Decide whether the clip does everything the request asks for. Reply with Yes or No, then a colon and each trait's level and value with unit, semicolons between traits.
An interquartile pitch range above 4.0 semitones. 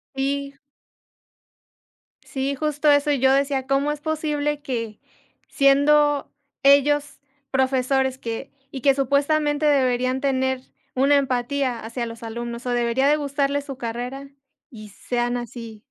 No: narrow, 2.6 semitones